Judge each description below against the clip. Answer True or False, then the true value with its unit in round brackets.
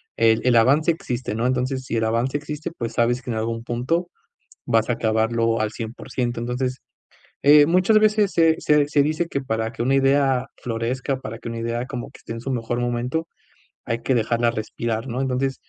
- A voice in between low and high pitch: False (125 Hz)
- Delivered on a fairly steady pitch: False (3.1 semitones)